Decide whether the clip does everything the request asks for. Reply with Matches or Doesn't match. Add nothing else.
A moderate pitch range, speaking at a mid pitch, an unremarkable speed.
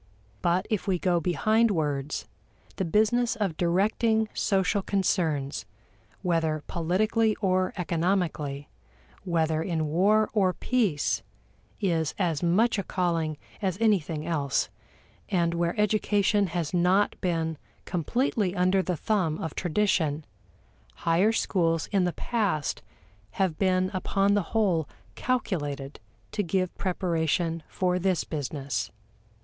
Doesn't match